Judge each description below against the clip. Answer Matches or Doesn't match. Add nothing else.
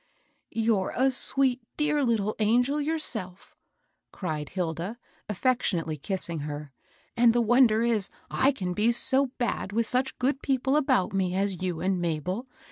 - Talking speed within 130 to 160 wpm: Matches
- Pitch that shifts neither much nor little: Doesn't match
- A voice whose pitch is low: Doesn't match